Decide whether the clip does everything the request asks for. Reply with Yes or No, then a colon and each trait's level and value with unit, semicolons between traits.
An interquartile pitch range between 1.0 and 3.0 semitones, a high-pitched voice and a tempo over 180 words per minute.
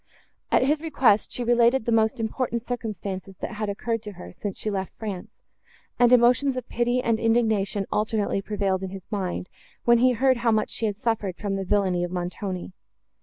No: average, 3.4 semitones; high, 220 Hz; average, 190 wpm